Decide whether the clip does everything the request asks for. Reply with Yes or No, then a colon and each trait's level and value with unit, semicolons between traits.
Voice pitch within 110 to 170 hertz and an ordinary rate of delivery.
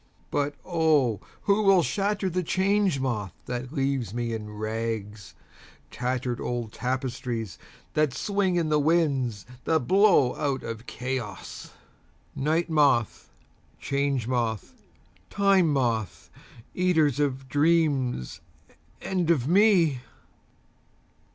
No: medium, 140 Hz; slow, 100 wpm